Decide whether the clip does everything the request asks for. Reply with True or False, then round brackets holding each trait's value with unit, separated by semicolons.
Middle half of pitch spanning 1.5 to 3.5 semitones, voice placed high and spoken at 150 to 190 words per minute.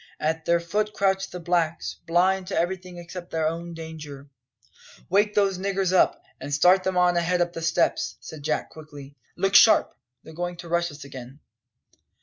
False (2.7 semitones; 175 Hz; 175 wpm)